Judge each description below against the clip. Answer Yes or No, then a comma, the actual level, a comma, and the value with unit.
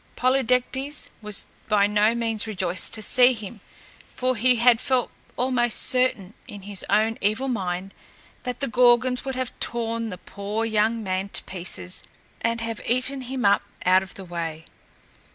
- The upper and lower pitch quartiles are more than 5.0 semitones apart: No, average, 3.9 semitones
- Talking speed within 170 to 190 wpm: No, average, 160 wpm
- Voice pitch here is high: Yes, high, 225 Hz